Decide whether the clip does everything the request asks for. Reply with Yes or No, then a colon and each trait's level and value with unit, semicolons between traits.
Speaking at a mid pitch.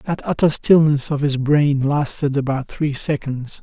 Yes: medium, 145 Hz